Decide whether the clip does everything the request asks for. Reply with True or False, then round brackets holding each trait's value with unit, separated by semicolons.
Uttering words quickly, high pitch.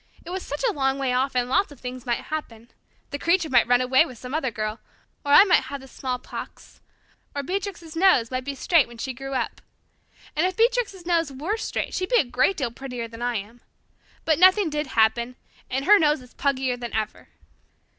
True (215 wpm; 270 Hz)